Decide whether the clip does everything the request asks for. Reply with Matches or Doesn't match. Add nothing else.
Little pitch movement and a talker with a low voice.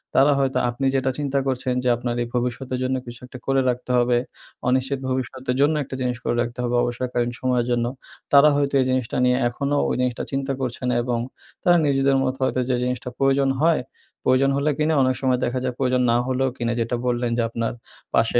Matches